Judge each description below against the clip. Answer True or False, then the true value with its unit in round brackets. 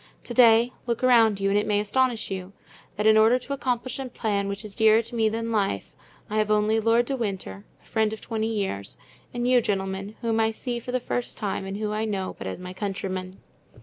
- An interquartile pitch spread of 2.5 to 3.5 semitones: True (2.9 semitones)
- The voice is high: True (220 Hz)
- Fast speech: True (230 wpm)